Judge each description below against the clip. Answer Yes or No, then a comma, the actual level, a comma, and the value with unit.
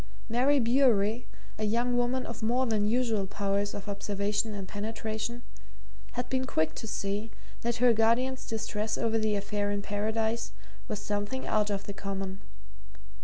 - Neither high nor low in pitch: No, high, 220 Hz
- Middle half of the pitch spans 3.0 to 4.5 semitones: No, narrow, 2.6 semitones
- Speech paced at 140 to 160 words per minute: Yes, average, 155 wpm